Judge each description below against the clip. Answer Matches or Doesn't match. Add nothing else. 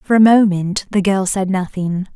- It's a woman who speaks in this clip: Matches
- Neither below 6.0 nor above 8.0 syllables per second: Doesn't match